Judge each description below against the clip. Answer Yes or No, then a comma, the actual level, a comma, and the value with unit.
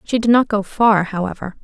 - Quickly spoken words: Yes, fast, 220 wpm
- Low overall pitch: No, high, 210 Hz